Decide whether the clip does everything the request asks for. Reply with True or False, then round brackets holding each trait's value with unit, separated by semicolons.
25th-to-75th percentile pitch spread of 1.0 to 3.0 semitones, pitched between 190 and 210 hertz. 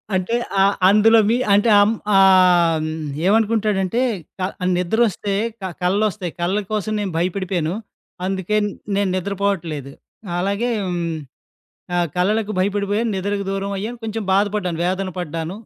True (2.7 semitones; 195 Hz)